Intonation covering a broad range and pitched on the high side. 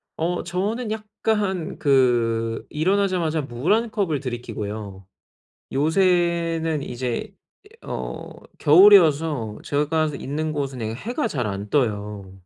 No: wide, 7.0 semitones; medium, 150 Hz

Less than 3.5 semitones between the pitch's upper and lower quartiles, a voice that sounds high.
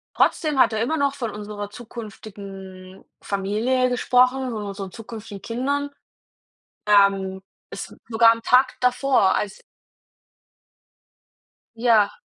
No: average, 3.9 semitones; high, 220 Hz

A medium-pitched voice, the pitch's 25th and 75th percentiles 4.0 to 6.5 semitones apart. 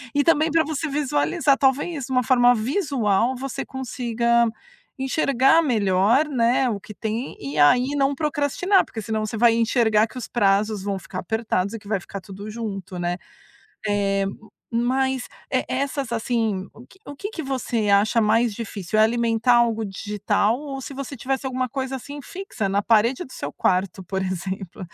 No: high, 235 Hz; average, 4.6 semitones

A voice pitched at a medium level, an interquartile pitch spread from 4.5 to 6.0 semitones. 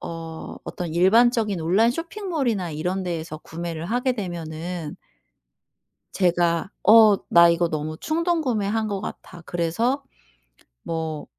Yes: medium, 180 Hz; wide, 5.5 semitones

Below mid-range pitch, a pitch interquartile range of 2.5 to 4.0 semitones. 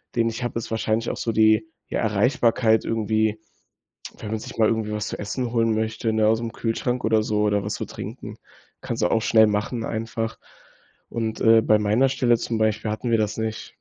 No: low, 110 Hz; narrow, 1.1 semitones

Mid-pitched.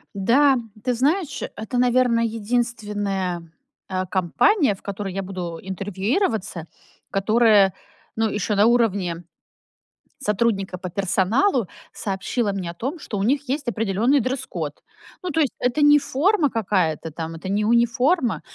No: high, 215 Hz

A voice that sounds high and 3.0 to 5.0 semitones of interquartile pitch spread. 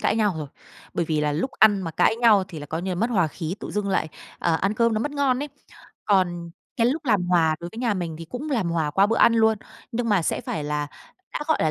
No: high, 195 Hz; wide, 5.6 semitones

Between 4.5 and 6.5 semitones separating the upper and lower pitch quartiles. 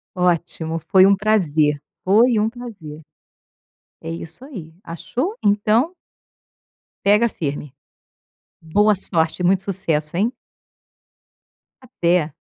Yes: average, 4.8 semitones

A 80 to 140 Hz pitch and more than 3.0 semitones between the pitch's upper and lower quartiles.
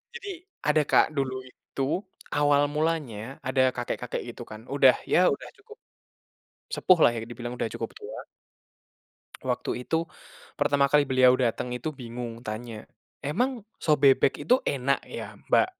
Yes: low, 135 Hz; average, 3.6 semitones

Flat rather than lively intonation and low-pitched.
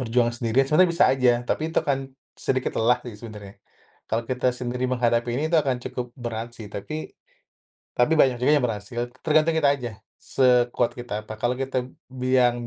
Yes: narrow, 2.1 semitones; low, 125 Hz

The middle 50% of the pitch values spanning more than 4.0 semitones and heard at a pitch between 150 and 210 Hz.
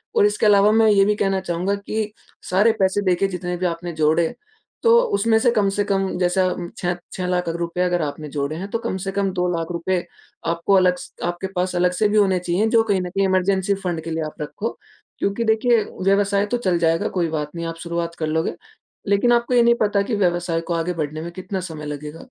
No: average, 3.1 semitones; medium, 185 Hz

